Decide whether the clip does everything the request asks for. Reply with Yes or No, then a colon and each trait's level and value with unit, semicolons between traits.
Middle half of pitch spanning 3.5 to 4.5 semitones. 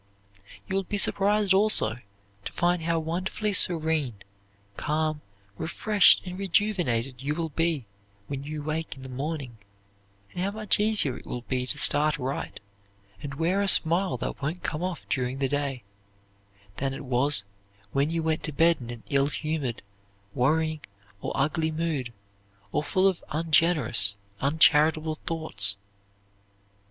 Yes: average, 3.9 semitones